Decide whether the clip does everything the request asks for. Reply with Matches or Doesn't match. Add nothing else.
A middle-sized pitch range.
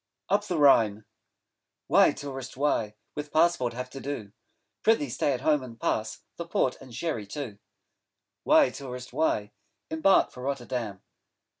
Matches